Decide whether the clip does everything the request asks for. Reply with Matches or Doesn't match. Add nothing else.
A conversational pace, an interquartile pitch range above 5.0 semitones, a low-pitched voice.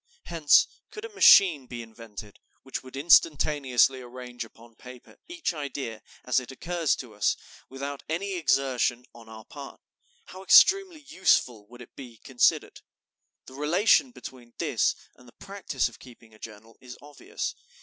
Matches